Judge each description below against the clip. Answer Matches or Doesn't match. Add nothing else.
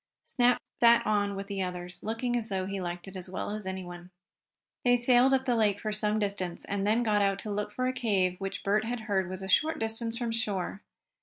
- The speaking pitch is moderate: Doesn't match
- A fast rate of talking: Matches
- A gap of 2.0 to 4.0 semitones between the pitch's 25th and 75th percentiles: Matches